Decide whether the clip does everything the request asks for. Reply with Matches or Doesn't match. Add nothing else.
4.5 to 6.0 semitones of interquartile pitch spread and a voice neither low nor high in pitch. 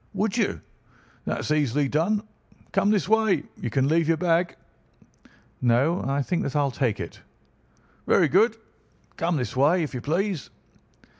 Matches